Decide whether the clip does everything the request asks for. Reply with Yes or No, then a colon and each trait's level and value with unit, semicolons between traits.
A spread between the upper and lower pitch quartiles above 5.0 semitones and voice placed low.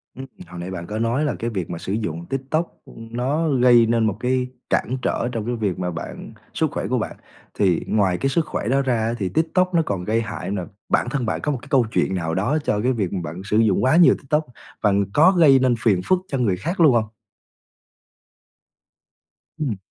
Yes: wide, 5.5 semitones; low, 115 Hz